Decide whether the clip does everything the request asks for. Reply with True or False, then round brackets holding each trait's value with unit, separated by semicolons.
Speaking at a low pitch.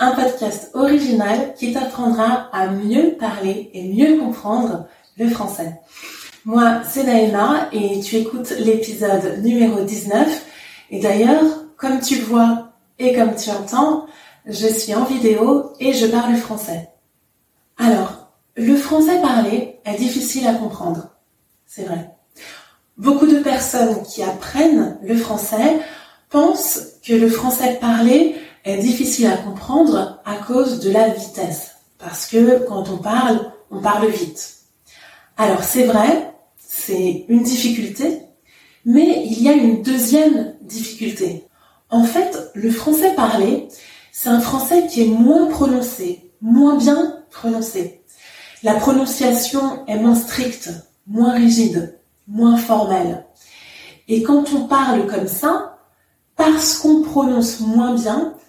False (235 Hz)